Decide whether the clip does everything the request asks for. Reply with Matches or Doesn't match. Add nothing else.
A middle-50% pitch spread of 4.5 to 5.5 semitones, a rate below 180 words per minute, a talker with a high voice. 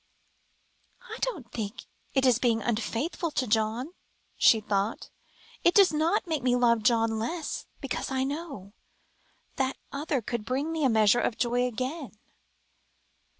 Matches